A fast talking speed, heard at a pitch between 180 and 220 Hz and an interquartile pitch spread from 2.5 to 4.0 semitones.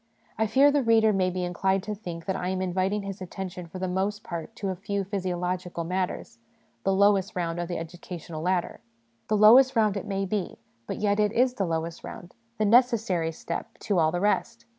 Yes: fast, 210 wpm; high, 190 Hz; average, 2.9 semitones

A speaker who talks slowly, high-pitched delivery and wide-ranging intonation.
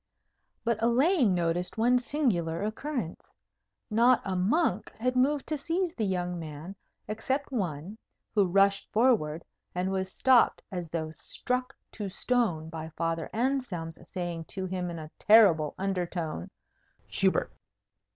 Yes: slow, 130 wpm; high, 195 Hz; wide, 6.4 semitones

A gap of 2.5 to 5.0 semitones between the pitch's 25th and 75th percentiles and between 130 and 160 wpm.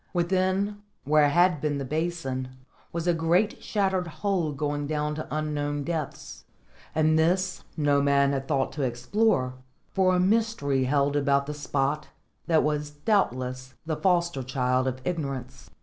Yes: average, 3.9 semitones; average, 150 wpm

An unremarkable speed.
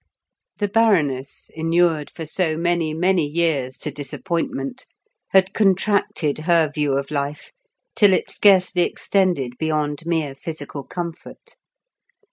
No: slow, 115 wpm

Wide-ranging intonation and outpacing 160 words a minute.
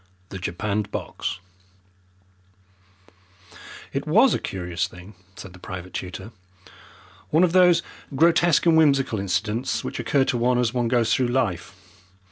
No: wide, 6.6 semitones; slow, 135 wpm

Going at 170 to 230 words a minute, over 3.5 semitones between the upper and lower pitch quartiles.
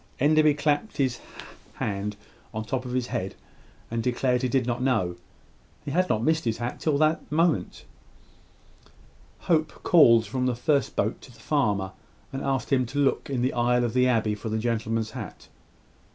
Yes: average, 180 wpm; average, 3.9 semitones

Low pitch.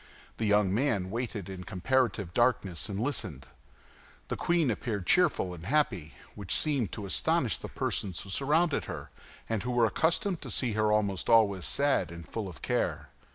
Yes: low, 110 Hz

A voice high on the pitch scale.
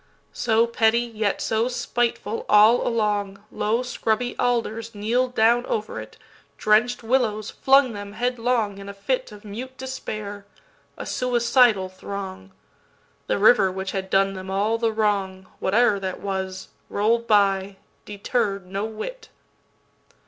Yes: high, 215 Hz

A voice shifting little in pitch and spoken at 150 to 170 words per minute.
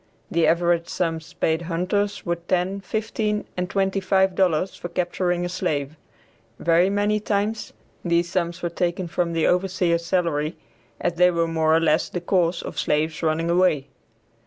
Yes: narrow, 2.2 semitones; average, 160 wpm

